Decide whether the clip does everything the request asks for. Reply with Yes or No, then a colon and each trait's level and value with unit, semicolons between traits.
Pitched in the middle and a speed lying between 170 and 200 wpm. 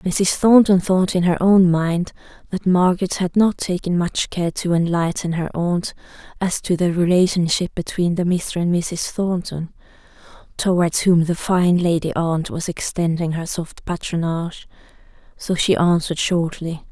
No: medium, 175 Hz; average, 155 wpm